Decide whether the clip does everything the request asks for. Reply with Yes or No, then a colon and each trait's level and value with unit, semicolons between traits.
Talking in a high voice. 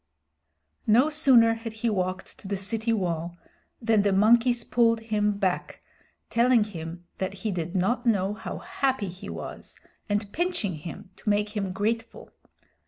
Yes: high, 210 Hz